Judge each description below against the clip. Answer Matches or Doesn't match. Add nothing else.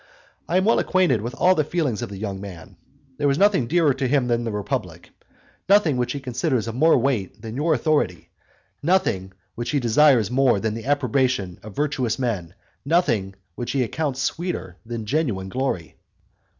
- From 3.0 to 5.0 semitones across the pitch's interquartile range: Doesn't match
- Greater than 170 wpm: Matches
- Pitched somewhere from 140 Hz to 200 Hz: Doesn't match